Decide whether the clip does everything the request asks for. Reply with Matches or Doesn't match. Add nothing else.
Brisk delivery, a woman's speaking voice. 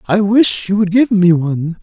Doesn't match